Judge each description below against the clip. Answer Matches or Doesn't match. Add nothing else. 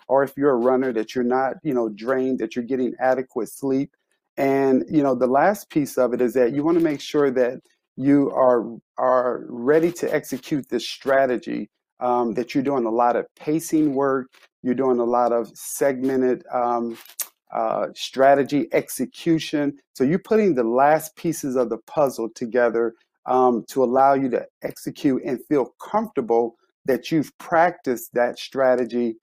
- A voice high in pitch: Doesn't match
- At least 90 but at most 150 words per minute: Doesn't match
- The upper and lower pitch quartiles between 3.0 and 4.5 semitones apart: Doesn't match